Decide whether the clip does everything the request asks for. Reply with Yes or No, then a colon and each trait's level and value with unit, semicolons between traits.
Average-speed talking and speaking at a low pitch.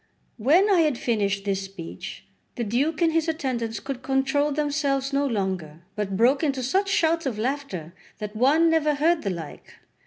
No: average, 175 wpm; very high, 270 Hz